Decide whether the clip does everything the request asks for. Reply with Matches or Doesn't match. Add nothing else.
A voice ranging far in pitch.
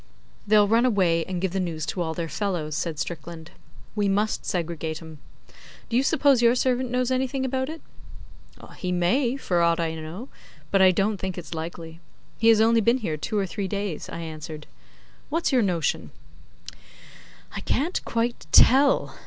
Matches